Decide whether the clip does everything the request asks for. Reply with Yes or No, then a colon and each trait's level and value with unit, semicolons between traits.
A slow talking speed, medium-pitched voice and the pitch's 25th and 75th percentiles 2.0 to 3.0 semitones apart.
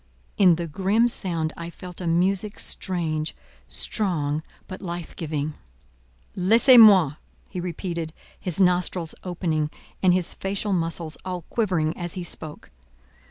Yes: slow, 130 wpm; medium, 175 Hz; narrow, 2.6 semitones